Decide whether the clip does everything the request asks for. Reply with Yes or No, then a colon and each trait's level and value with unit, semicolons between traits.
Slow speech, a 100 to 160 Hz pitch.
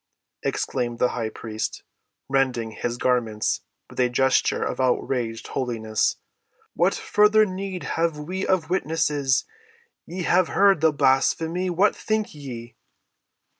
Yes: slow, 125 wpm; low, 135 Hz